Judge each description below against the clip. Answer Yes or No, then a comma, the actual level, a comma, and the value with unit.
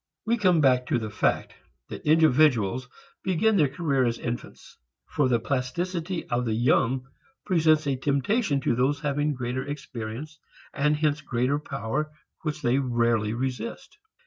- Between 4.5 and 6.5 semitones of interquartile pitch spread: No, average, 3.8 semitones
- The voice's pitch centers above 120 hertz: Yes, medium, 140 Hz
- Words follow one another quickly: No, average, 145 wpm